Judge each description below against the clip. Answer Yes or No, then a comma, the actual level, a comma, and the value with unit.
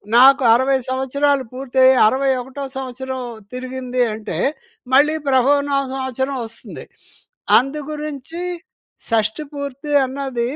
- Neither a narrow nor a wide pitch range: No, narrow, 1.7 semitones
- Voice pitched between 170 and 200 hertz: No, very high, 265 Hz